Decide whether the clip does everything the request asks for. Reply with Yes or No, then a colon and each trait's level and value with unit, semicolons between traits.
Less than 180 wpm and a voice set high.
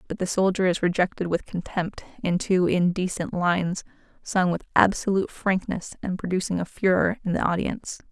No: average, 165 wpm; medium, 180 Hz